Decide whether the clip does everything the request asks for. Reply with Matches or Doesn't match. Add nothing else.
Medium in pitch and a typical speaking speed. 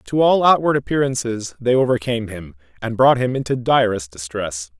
Doesn't match